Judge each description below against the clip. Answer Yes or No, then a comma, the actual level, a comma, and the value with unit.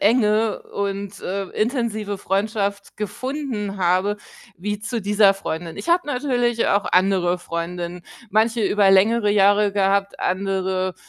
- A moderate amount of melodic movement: No, narrow, 2.2 semitones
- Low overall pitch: No, high, 200 Hz